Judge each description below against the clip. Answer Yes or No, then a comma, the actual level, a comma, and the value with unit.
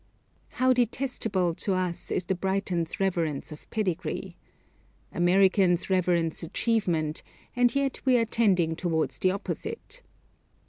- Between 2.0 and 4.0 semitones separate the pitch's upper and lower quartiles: No, average, 4.8 semitones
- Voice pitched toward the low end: No, medium, 185 Hz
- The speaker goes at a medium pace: No, slow, 120 wpm